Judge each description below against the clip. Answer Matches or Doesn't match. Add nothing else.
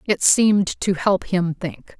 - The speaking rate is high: Doesn't match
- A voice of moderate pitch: Matches